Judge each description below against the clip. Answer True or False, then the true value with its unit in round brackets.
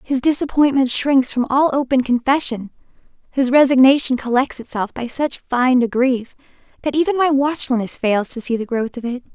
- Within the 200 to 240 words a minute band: False (165 wpm)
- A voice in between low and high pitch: False (260 Hz)